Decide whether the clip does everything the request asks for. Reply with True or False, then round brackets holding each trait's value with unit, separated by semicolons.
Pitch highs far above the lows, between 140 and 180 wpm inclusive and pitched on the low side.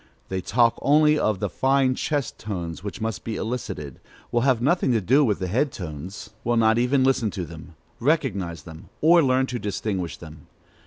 False (6.3 semitones; 190 wpm; 110 Hz)